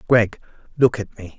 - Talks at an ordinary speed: Yes, average, 175 wpm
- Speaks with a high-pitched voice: No, low, 110 Hz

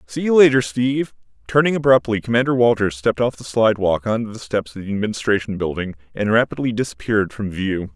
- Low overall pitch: Yes, low, 110 Hz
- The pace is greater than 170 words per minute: Yes, average, 180 wpm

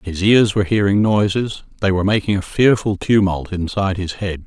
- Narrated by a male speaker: Yes, male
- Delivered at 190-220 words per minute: No, average, 175 wpm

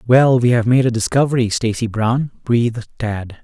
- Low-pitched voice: Yes, low, 120 Hz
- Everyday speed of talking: Yes, average, 175 wpm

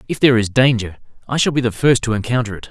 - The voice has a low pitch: Yes, low, 120 Hz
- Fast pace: Yes, fast, 265 wpm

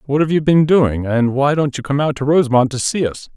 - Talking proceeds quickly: Yes, fast, 285 wpm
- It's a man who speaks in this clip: Yes, male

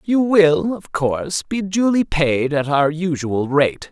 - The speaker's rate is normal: Yes, average, 170 wpm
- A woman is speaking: No, male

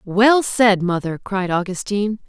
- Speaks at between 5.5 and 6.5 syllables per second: No, 4.3 syllables/s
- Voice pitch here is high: Yes, high, 200 Hz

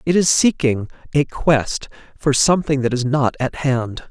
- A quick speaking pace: No, average, 175 wpm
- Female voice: No, male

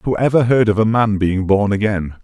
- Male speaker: Yes, male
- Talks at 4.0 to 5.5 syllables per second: Yes, 5.1 syllables/s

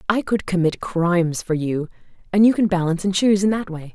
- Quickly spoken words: Yes, fast, 215 wpm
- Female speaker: Yes, female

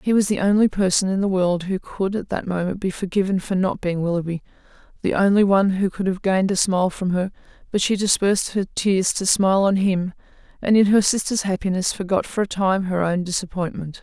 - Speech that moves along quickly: Yes, fast, 220 wpm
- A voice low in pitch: No, high, 190 Hz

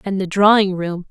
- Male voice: No, female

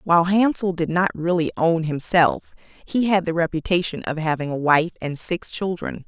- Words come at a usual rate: Yes, average, 180 wpm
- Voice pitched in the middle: Yes, medium, 170 Hz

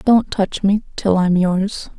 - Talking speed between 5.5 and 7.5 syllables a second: No, 3.5 syllables/s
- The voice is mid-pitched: No, high, 195 Hz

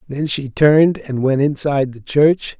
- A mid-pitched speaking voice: Yes, medium, 145 Hz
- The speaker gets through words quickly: No, average, 185 wpm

